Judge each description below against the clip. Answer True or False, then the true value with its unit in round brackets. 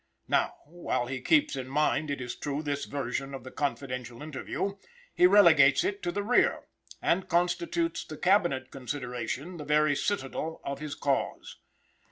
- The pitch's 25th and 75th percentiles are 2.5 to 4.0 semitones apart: False (4.6 semitones)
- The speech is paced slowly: False (160 wpm)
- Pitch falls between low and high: True (145 Hz)